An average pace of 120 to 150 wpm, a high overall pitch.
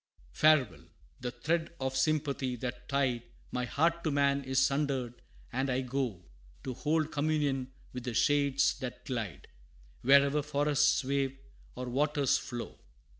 No: average, 140 wpm; low, 135 Hz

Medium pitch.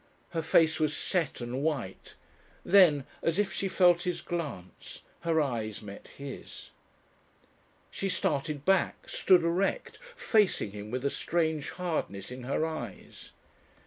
Yes: medium, 160 Hz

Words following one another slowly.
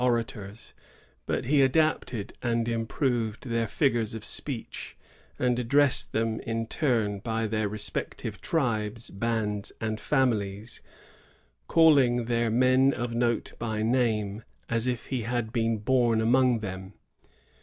Yes: slow, 130 wpm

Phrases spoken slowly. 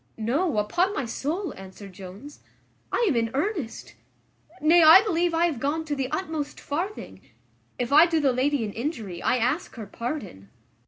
No: average, 170 wpm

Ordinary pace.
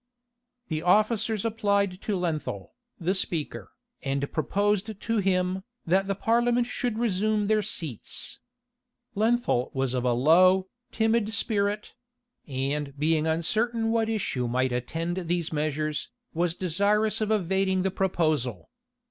No: slow, 125 wpm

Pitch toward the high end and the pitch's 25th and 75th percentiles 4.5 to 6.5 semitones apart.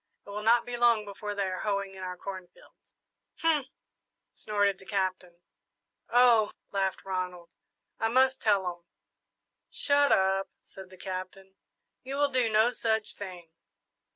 No: high, 200 Hz; average, 3.7 semitones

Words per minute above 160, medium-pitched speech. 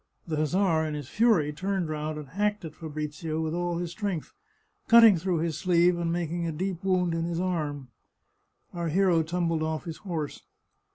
Yes: average, 180 wpm; medium, 170 Hz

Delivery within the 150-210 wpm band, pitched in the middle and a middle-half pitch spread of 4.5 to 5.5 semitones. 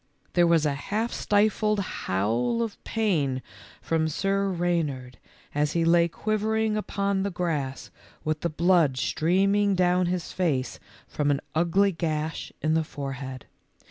No: average, 140 wpm; medium, 170 Hz; average, 5.0 semitones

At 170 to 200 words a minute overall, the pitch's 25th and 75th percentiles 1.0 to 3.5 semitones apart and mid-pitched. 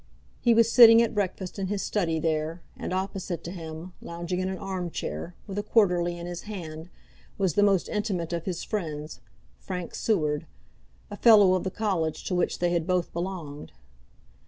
Yes: average, 180 wpm; average, 3.0 semitones; medium, 180 Hz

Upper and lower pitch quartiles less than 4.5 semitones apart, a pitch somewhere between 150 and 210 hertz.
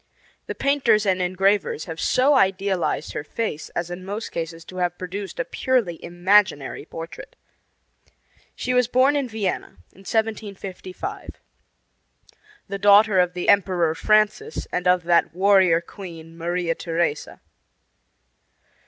Yes: average, 3.6 semitones; high, 190 Hz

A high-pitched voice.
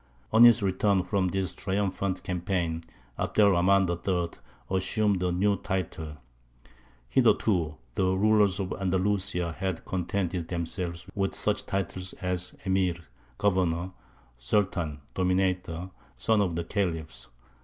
No: very low, 95 Hz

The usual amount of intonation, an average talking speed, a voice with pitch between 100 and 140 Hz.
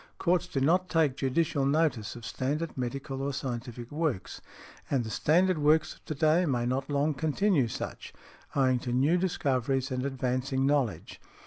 Yes: average, 3.5 semitones; average, 160 wpm; low, 135 Hz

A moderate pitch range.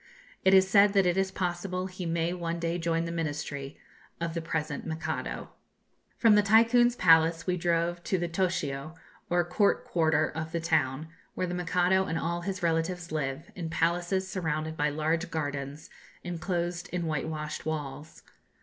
No: narrow, 2.2 semitones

